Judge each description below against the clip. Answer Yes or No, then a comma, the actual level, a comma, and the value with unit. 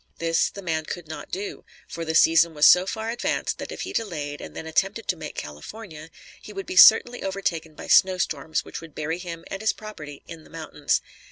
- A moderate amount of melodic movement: Yes, average, 3.6 semitones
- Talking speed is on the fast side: Yes, fast, 215 wpm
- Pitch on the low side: No, medium, 165 Hz